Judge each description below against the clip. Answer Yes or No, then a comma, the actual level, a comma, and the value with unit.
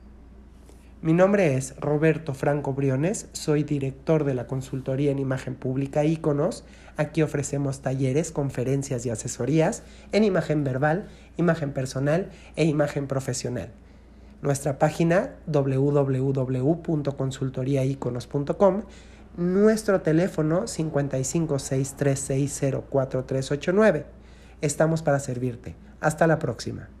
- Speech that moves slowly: Yes, slow, 90 wpm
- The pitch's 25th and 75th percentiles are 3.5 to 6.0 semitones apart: No, average, 3.1 semitones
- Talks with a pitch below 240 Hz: Yes, medium, 140 Hz